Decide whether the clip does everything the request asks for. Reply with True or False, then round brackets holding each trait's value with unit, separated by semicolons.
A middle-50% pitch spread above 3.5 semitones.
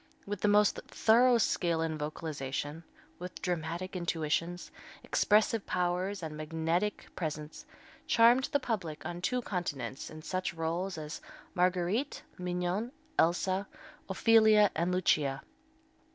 True (4.2 semitones)